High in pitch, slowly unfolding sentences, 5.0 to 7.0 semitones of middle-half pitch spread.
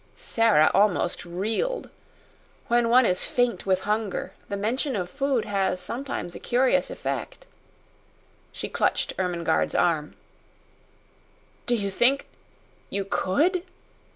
Yes: high, 210 Hz; slow, 115 wpm; average, 5.3 semitones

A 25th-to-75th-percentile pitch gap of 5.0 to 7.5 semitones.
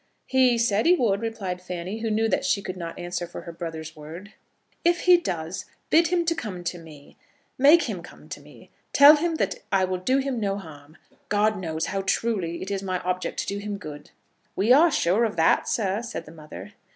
Yes: wide, 5.4 semitones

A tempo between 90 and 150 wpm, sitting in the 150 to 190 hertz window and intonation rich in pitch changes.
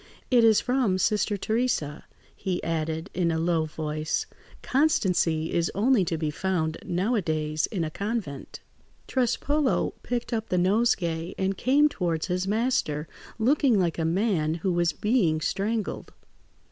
Yes: average, 140 wpm; medium, 185 Hz; wide, 6.0 semitones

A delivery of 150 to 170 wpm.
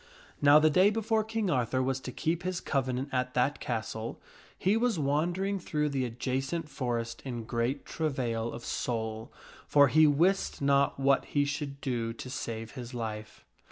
Yes: average, 165 wpm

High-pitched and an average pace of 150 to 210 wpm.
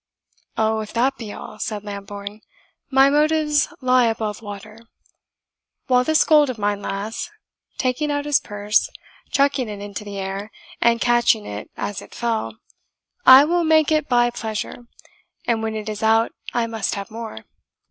Yes: high, 225 Hz; average, 160 wpm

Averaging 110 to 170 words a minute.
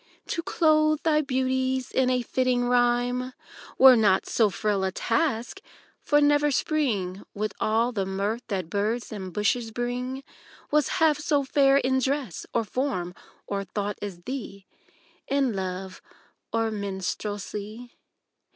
Yes: slow, 135 wpm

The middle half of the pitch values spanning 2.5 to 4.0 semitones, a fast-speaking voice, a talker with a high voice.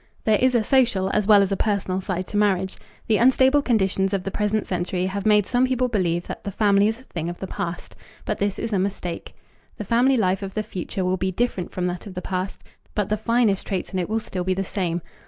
Yes: average, 2.8 semitones; fast, 250 wpm; high, 200 Hz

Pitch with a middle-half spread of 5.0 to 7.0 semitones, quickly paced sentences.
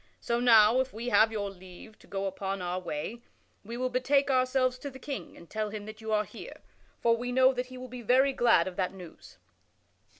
No: average, 4.4 semitones; fast, 225 wpm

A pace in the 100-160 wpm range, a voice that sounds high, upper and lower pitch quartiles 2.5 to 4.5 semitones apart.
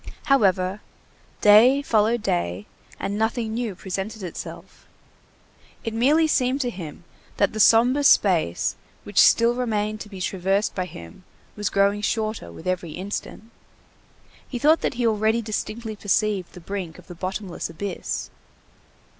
Yes: average, 140 wpm; high, 210 Hz; average, 3.7 semitones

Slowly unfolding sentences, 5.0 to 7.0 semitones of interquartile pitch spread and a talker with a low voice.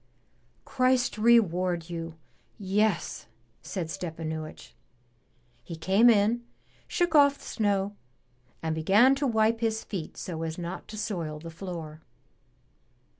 No: slow, 120 wpm; wide, 5.5 semitones; high, 195 Hz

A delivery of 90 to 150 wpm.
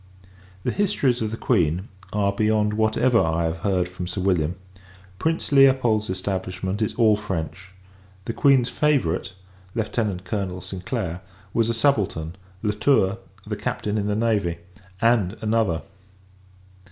Yes: average, 140 wpm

